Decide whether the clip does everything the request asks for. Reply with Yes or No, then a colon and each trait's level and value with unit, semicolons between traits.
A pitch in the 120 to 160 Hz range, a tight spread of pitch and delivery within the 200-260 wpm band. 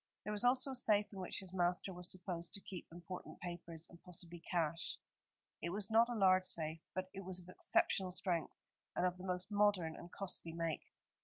No: medium, 180 Hz; narrow, 2.2 semitones; fast, 205 wpm